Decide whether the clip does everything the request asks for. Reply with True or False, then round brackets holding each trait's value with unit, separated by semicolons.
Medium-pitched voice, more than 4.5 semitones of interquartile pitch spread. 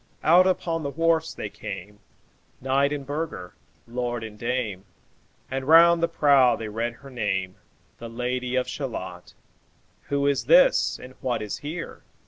False (130 Hz; 5.2 semitones)